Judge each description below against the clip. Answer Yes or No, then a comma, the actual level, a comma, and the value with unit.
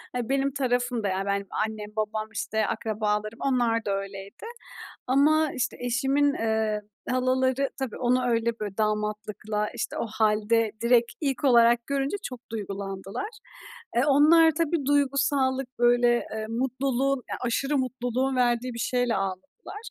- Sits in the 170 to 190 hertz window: No, high, 240 Hz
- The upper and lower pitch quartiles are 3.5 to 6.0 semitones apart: Yes, average, 3.8 semitones